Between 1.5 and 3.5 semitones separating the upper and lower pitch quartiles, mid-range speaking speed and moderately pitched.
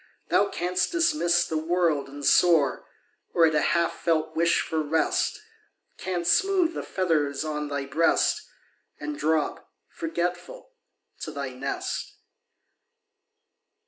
No: average, 3.1 semitones; slow, 120 wpm; medium, 165 Hz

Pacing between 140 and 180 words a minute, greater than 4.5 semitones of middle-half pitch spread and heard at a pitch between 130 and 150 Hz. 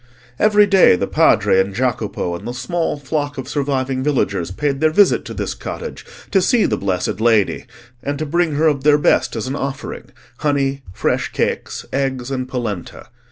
No: average, 175 wpm; average, 3.9 semitones; low, 135 Hz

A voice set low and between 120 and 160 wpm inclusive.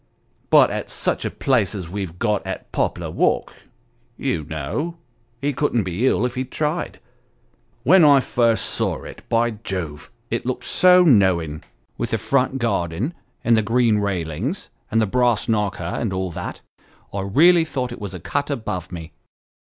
No: low, 110 Hz; average, 170 wpm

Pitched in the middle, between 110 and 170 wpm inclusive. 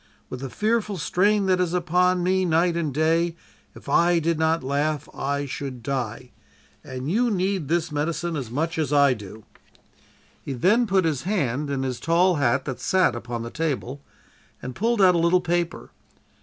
No: medium, 160 Hz; average, 180 wpm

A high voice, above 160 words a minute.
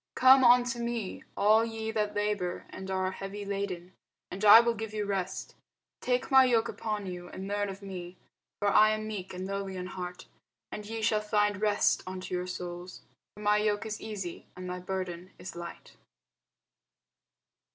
Yes: high, 205 Hz; average, 175 wpm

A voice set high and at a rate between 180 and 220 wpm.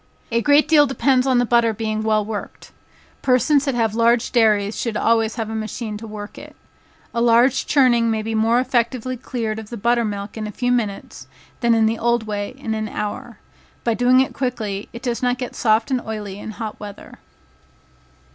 Yes: high, 230 Hz; average, 200 wpm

